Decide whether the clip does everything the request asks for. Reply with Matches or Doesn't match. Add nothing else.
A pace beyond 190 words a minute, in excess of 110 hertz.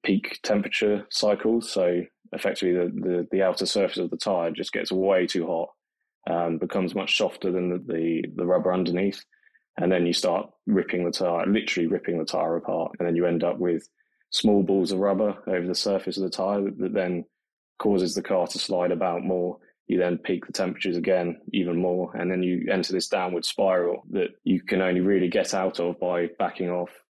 Doesn't match